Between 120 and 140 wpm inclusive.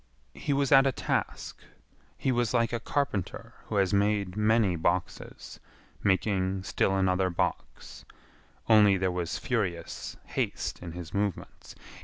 Yes: slow, 135 wpm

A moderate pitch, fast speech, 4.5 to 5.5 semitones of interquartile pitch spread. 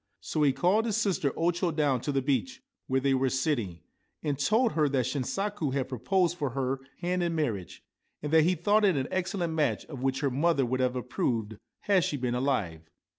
Yes: medium, 145 Hz; fast, 210 wpm; average, 5.2 semitones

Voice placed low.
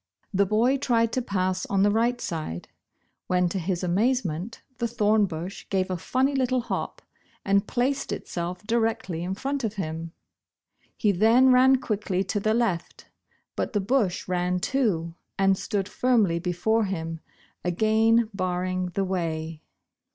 No: high, 200 Hz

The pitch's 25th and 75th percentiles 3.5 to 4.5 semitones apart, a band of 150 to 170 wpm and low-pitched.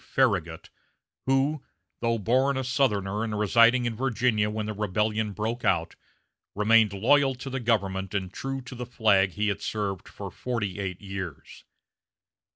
Yes: average, 4.0 semitones; average, 155 wpm; low, 110 Hz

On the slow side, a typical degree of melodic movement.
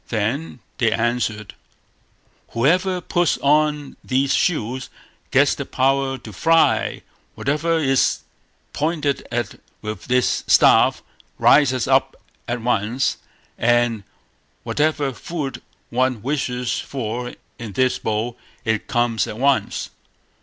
Yes: slow, 110 wpm; average, 3.6 semitones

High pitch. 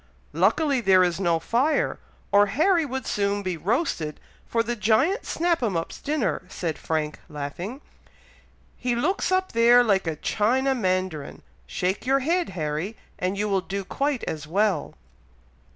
Yes: high, 210 Hz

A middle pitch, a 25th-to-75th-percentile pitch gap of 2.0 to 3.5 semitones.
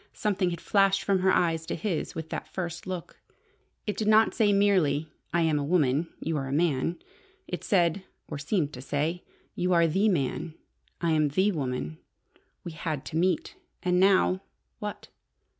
No: medium, 170 Hz; average, 3.9 semitones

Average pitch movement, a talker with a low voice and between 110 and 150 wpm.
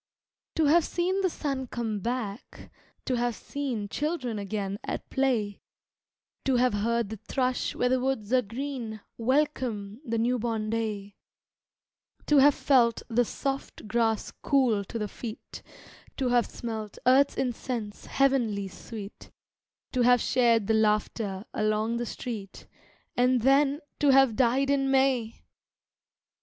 No: average, 3.6 semitones; high, 240 Hz; average, 140 wpm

